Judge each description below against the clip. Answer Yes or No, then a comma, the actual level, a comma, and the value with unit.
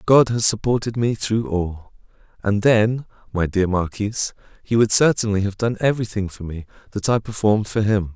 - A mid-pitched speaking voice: No, low, 105 Hz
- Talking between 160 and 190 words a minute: Yes, average, 175 wpm